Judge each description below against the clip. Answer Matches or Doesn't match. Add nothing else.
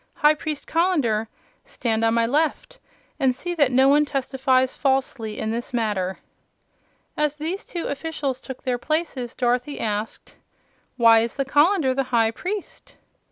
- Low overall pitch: Doesn't match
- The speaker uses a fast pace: Doesn't match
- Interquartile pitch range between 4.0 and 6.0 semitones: Matches